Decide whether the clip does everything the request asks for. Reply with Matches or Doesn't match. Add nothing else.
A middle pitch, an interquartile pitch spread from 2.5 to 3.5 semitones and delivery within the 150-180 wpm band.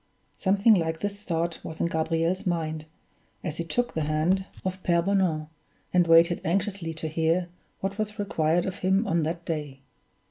Matches